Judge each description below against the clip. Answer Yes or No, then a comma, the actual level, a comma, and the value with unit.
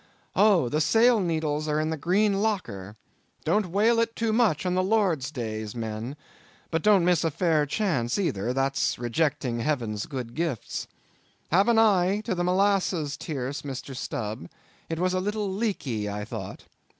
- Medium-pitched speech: Yes, medium, 160 Hz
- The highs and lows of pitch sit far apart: Yes, wide, 7.6 semitones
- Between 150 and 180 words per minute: Yes, average, 160 wpm